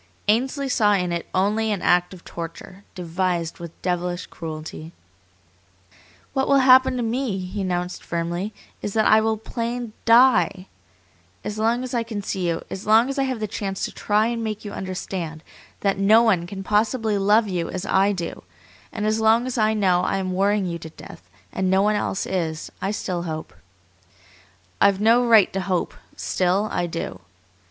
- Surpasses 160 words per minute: Yes, average, 185 wpm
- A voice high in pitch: Yes, high, 200 Hz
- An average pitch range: Yes, average, 3.7 semitones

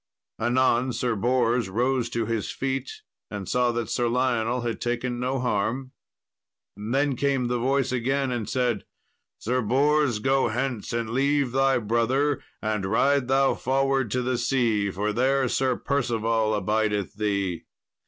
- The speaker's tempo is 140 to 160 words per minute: Yes, average, 145 wpm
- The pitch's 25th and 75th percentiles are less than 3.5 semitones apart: Yes, average, 2.9 semitones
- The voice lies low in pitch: Yes, low, 120 Hz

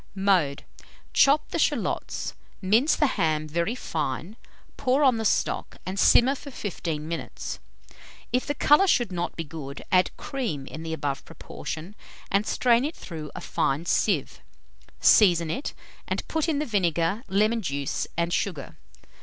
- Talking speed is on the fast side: No, average, 155 wpm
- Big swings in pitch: Yes, wide, 7.2 semitones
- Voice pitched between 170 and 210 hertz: Yes, medium, 185 Hz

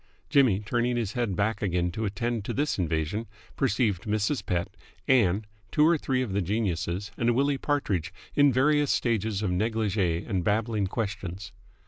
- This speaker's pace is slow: No, average, 160 wpm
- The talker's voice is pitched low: Yes, low, 110 Hz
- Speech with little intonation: No, average, 4.1 semitones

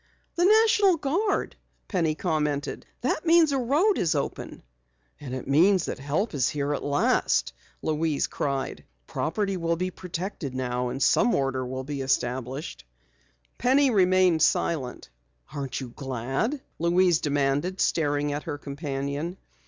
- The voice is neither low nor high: Yes, medium, 155 Hz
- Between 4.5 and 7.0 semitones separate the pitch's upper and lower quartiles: Yes, wide, 5.6 semitones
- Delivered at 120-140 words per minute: Yes, slow, 135 wpm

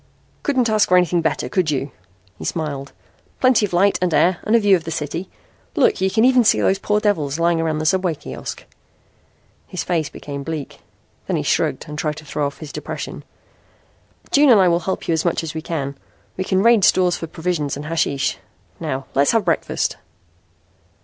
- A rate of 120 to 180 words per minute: No, average, 200 wpm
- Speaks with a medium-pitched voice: Yes, medium, 170 Hz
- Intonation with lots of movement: No, average, 4.1 semitones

